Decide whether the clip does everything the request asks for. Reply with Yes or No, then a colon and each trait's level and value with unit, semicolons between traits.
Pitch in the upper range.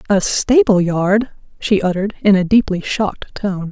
Yes: high, 200 Hz